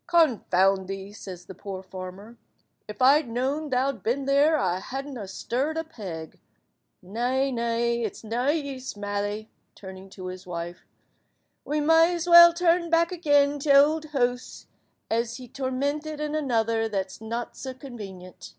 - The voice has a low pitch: No, high, 245 Hz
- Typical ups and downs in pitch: No, wide, 6.3 semitones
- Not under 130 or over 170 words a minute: Yes, average, 155 wpm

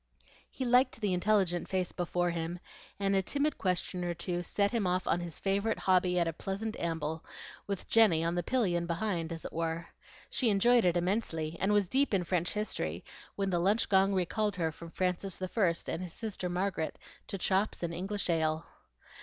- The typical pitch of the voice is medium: Yes, medium, 180 Hz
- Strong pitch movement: No, average, 2.9 semitones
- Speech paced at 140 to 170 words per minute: No, average, 190 wpm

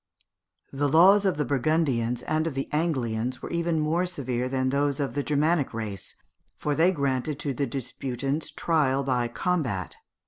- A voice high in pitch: No, medium, 140 Hz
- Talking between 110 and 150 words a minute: No, average, 160 wpm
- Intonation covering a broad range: No, average, 3.7 semitones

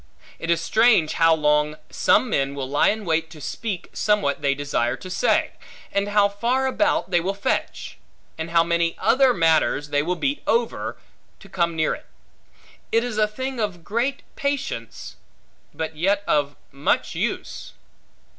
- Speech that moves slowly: No, average, 165 wpm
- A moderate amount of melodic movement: No, wide, 6.2 semitones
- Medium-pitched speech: Yes, medium, 175 Hz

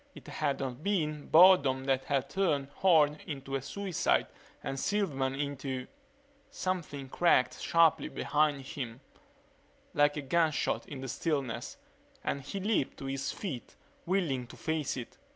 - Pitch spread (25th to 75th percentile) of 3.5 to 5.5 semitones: Yes, average, 3.8 semitones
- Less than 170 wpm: Yes, average, 140 wpm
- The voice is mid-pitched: Yes, medium, 145 Hz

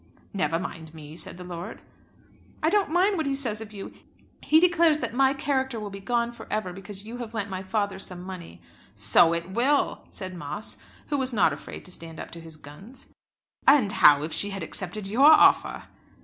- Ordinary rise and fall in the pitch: No, wide, 6.9 semitones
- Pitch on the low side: No, high, 200 Hz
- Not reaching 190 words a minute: No, fast, 205 wpm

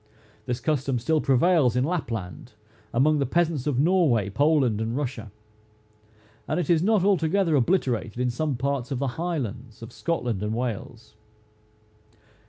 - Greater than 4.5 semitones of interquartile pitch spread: Yes, average, 5.2 semitones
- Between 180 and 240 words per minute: No, average, 145 wpm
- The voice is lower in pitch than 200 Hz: Yes, low, 135 Hz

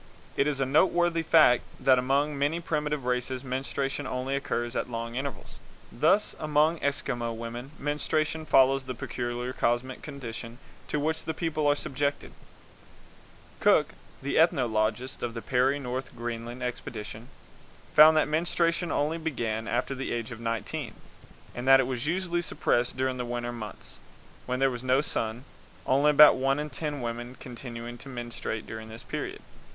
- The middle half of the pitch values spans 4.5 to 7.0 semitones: No, average, 3.7 semitones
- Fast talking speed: No, average, 155 wpm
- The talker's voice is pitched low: Yes, low, 130 Hz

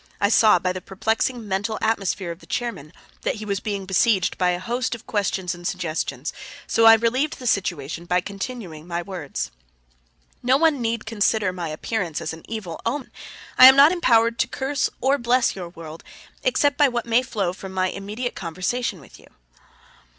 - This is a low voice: No, high, 205 Hz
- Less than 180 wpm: No, average, 185 wpm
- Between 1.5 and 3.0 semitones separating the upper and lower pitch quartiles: No, average, 4.9 semitones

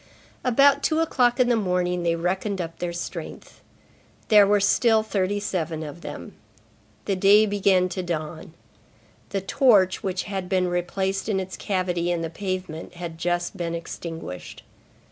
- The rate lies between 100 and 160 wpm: Yes, average, 155 wpm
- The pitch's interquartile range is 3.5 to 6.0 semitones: No, average, 2.8 semitones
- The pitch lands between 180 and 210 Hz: Yes, medium, 185 Hz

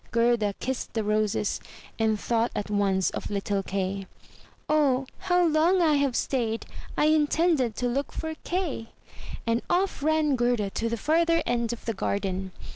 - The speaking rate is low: No, average, 160 wpm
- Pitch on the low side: No, high, 240 Hz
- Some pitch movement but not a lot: No, wide, 6.5 semitones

